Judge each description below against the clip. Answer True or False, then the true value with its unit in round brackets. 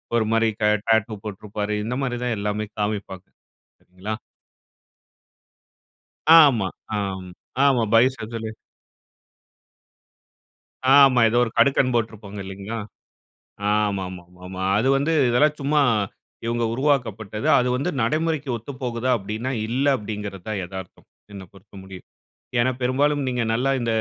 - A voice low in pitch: True (115 Hz)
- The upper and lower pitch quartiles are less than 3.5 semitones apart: False (3.9 semitones)